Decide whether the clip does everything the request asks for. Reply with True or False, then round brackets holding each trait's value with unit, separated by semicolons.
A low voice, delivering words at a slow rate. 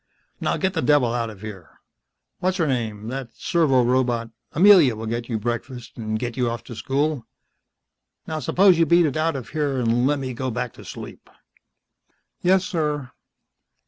False (130 Hz; 175 wpm)